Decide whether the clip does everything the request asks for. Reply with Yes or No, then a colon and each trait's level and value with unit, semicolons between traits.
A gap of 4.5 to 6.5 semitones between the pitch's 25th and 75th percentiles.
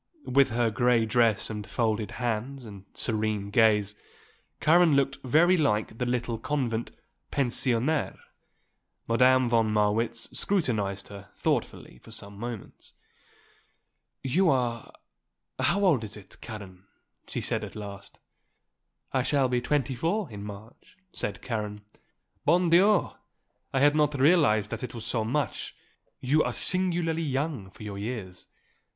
Yes: average, 5.1 semitones